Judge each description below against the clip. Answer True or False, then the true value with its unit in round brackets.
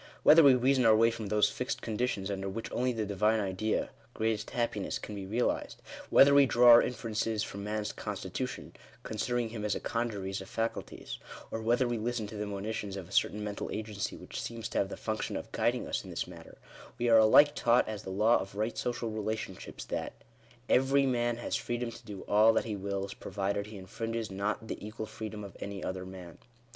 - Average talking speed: False (220 wpm)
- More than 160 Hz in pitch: False (110 Hz)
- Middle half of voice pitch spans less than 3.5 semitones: True (2.8 semitones)